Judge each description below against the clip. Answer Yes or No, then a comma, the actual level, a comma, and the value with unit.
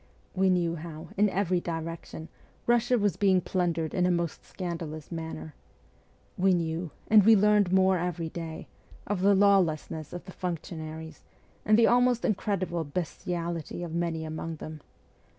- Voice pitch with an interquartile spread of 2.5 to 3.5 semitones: Yes, average, 3.0 semitones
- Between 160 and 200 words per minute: No, average, 150 wpm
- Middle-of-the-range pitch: Yes, medium, 175 Hz